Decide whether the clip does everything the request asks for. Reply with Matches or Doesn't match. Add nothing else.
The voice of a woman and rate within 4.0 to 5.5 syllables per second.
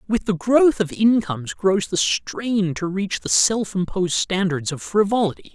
Doesn't match